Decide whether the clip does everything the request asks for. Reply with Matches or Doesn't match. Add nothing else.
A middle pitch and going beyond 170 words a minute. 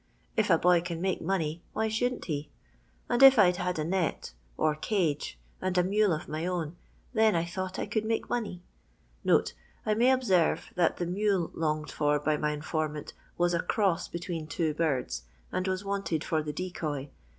Matches